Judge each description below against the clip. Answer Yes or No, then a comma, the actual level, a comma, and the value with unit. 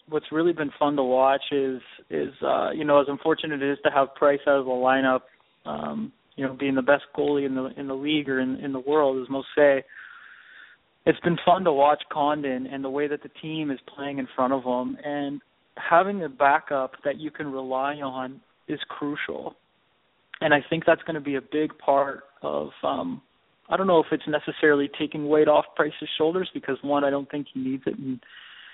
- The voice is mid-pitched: Yes, medium, 145 Hz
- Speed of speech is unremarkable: No, fast, 215 wpm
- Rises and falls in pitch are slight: Yes, narrow, 2.1 semitones